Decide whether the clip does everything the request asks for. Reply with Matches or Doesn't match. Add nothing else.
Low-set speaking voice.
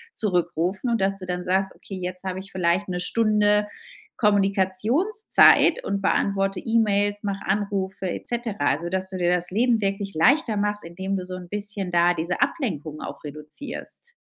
Doesn't match